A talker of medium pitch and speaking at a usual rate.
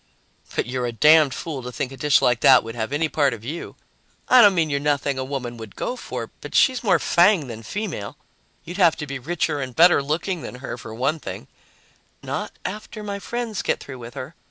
No: medium, 145 Hz; fast, 230 wpm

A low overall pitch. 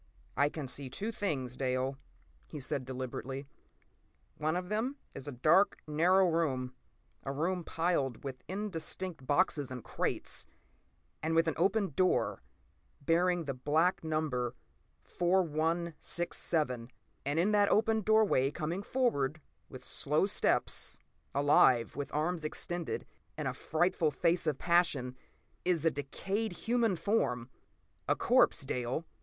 No: medium, 160 Hz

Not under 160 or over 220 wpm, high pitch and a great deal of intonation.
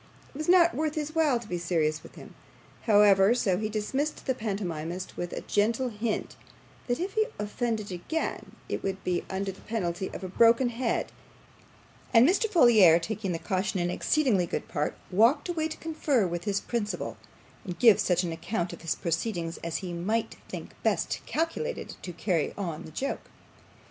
Yes: average, 180 wpm; high, 210 Hz; wide, 6.1 semitones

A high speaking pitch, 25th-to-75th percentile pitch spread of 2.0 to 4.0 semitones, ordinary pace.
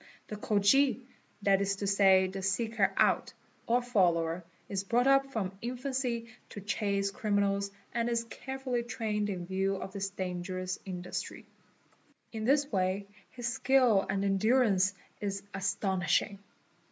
No: high, 200 Hz; average, 3.6 semitones; slow, 130 wpm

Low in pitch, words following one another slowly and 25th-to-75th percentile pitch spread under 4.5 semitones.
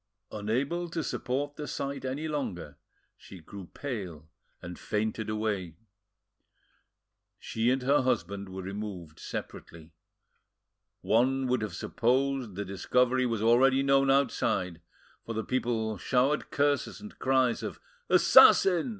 No: low, 120 Hz; slow, 125 wpm; average, 5.2 semitones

